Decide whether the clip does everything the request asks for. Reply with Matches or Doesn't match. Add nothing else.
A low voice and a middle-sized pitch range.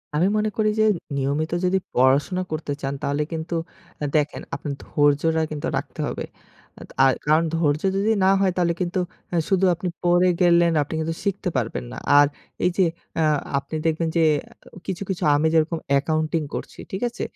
Doesn't match